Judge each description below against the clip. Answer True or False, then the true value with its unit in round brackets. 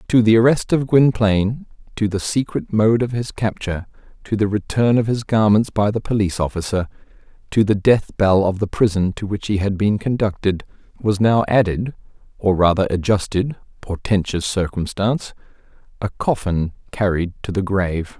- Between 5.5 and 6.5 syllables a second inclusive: False (5.1 syllables/s)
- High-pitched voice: False (105 Hz)